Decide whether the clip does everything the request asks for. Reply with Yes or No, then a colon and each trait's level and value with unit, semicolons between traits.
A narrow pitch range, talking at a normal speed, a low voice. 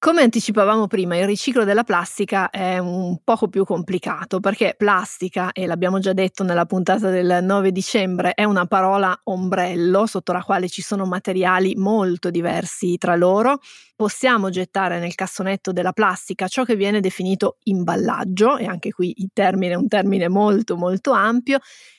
No: narrow, 2.2 semitones; average, 160 wpm; high, 190 Hz